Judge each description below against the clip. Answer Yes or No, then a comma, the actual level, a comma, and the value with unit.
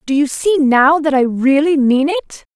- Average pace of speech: No, fast, 210 wpm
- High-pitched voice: Yes, very high, 290 Hz